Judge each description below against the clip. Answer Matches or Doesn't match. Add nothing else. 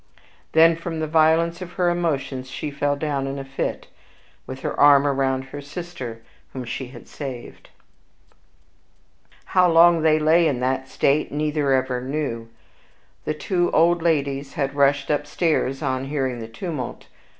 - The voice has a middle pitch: Matches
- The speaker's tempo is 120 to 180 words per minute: Matches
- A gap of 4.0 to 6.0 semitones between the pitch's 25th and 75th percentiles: Doesn't match